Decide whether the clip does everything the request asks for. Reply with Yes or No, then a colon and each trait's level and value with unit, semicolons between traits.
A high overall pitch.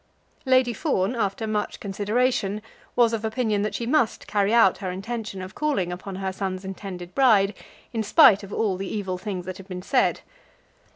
Yes: high, 205 Hz